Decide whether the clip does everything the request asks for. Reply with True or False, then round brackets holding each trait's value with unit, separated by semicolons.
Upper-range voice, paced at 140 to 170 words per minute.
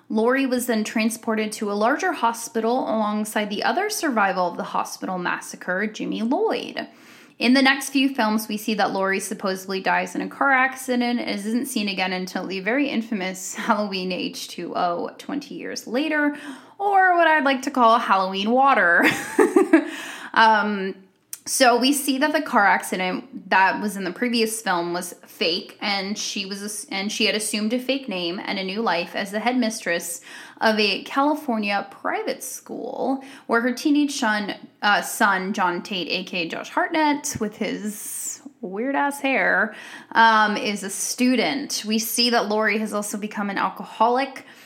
True (230 Hz; 165 wpm)